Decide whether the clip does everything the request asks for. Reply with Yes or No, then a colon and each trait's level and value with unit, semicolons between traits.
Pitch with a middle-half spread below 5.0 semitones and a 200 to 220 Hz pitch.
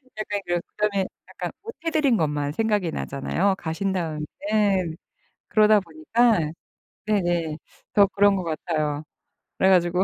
No: average, 4.4 semitones; high, 190 Hz